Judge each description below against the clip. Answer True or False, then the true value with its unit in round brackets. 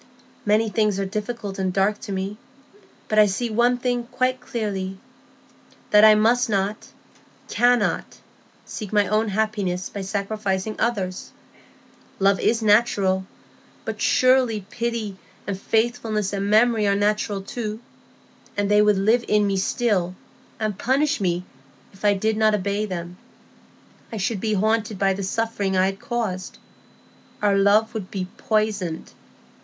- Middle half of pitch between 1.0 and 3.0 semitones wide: True (2.4 semitones)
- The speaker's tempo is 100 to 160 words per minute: True (140 wpm)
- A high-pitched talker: True (210 Hz)